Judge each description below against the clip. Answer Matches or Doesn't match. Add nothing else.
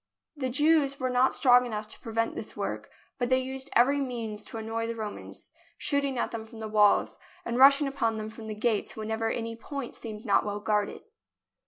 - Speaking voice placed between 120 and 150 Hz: Doesn't match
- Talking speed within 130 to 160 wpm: Doesn't match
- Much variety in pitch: Doesn't match